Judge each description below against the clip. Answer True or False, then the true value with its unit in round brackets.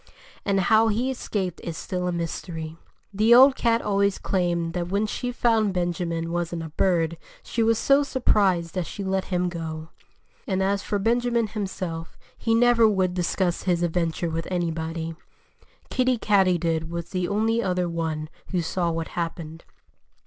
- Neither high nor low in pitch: True (180 Hz)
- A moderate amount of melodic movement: True (4.0 semitones)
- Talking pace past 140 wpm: True (160 wpm)